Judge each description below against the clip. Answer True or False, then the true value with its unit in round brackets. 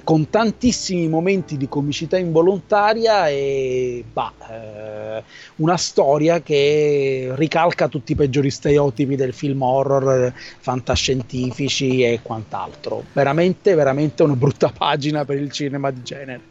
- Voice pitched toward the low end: False (145 Hz)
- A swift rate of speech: False (120 wpm)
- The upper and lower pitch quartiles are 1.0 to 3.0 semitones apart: False (3.7 semitones)